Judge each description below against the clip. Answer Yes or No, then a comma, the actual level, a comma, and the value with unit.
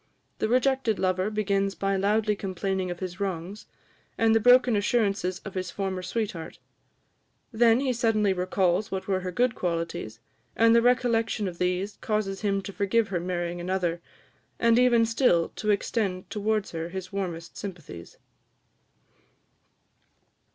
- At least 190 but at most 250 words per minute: No, average, 145 wpm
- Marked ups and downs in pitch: No, average, 3.5 semitones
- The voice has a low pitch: No, high, 195 Hz